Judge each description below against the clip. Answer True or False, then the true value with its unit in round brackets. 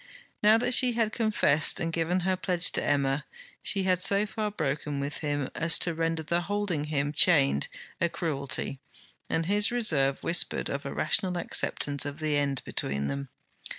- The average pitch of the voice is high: False (165 Hz)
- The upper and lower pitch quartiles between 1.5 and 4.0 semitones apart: False (4.8 semitones)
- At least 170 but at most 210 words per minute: True (175 wpm)